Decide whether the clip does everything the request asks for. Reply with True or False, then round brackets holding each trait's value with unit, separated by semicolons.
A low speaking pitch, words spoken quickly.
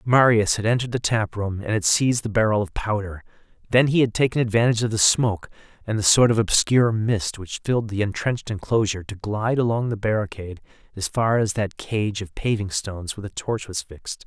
True (105 Hz; 210 wpm)